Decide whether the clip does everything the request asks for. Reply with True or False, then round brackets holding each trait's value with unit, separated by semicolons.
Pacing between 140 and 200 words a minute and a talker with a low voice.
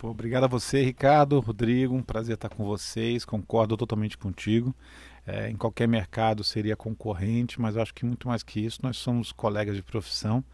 True (180 wpm; 115 Hz)